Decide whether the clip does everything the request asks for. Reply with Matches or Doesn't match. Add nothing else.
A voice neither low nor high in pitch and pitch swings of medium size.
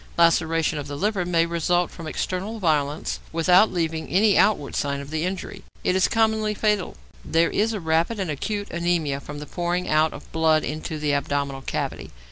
Matches